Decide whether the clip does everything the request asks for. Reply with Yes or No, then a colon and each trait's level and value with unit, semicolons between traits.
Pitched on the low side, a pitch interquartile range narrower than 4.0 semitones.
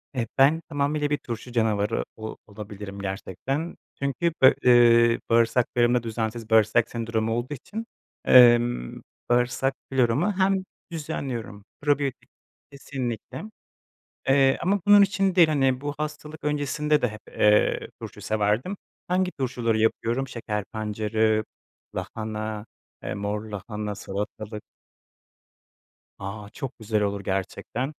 No: low, 120 Hz; average, 4.6 semitones